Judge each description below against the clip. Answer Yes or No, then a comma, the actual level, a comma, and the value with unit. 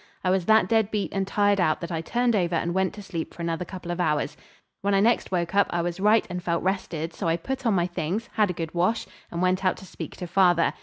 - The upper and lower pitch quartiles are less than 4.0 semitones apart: Yes, average, 2.9 semitones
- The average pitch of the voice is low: No, medium, 185 Hz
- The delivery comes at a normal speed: No, fast, 270 wpm